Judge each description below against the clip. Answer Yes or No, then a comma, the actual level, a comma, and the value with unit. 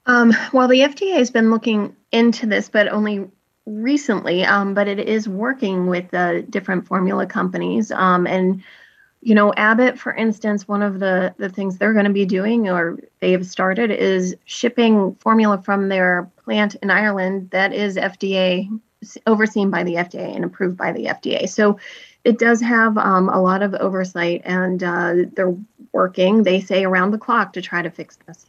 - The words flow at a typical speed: Yes, average, 185 wpm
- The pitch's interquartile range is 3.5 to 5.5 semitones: No, average, 3.1 semitones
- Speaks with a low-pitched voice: No, high, 200 Hz